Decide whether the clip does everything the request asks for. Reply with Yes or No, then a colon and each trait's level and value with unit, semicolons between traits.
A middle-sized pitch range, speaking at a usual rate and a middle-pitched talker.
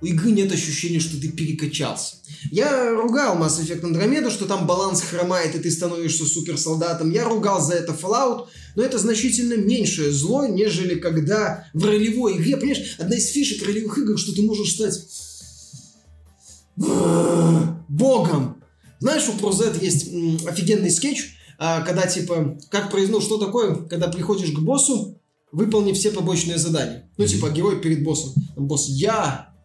Yes: average, 4.9 semitones; average, 150 wpm; medium, 175 Hz